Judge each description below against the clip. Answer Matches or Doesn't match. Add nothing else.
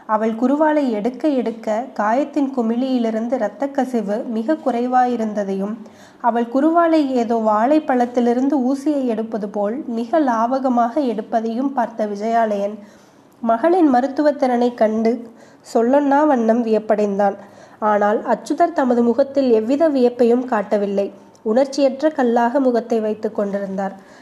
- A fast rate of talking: Doesn't match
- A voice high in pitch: Matches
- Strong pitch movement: Doesn't match